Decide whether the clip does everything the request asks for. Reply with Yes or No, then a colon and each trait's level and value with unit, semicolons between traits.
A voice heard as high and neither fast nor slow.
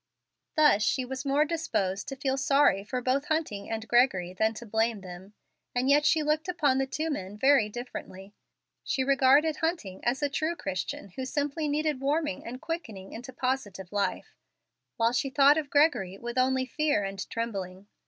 Yes: very high, 260 Hz; average, 175 wpm